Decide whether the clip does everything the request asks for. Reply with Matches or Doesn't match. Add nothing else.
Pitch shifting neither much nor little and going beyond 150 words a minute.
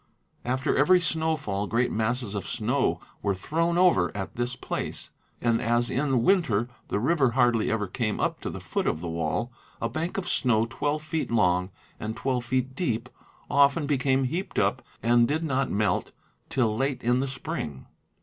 Matches